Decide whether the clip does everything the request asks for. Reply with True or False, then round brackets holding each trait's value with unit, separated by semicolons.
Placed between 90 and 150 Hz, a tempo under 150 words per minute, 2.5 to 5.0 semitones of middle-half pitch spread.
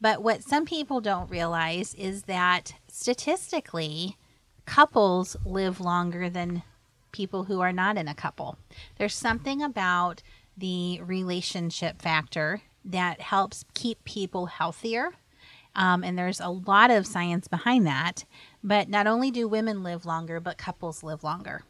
False (185 Hz; 140 wpm; 3.3 semitones)